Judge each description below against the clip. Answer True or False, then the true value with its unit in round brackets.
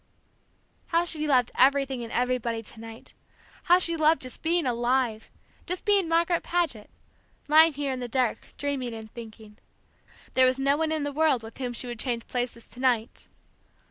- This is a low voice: False (260 Hz)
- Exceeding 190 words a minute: False (175 wpm)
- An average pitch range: True (4.7 semitones)